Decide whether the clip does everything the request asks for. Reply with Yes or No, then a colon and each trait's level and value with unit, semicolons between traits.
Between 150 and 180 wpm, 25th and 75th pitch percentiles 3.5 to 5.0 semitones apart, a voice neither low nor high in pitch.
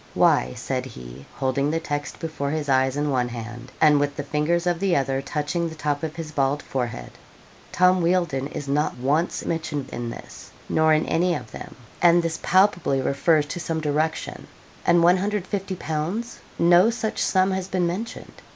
Yes: average, 175 wpm; average, 3.9 semitones; medium, 155 Hz